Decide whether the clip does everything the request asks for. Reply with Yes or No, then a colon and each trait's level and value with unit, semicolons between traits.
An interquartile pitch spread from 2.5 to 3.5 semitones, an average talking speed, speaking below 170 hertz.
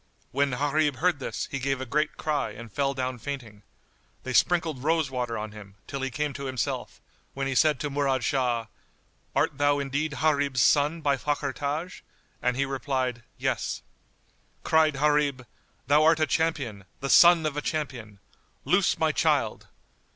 Yes: average, 2.8 semitones; average, 165 wpm; medium, 140 Hz